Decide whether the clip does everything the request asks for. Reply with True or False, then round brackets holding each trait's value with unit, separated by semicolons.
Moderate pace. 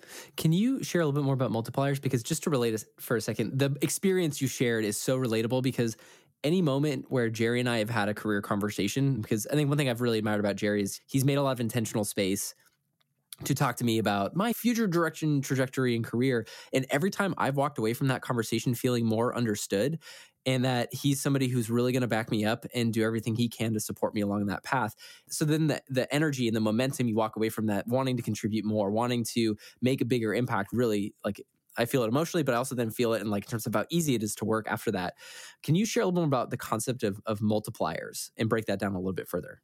False (250 wpm)